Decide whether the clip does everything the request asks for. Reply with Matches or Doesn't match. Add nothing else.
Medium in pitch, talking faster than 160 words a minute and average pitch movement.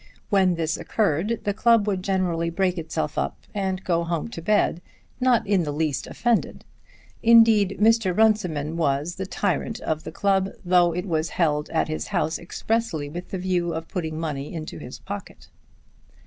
Matches